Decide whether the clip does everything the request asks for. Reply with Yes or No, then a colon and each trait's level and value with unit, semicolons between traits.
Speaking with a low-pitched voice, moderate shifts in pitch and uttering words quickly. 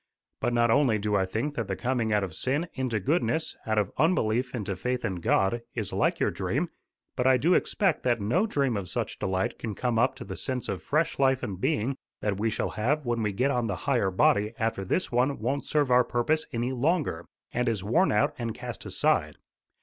Yes: low, 120 Hz; average, 4.3 semitones; fast, 220 wpm